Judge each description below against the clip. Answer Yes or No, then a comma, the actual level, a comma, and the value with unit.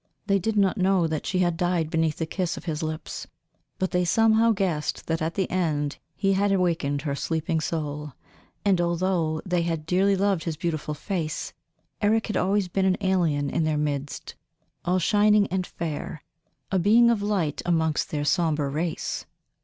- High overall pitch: No, medium, 175 Hz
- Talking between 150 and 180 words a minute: Yes, average, 175 wpm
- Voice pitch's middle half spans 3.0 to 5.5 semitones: Yes, average, 3.6 semitones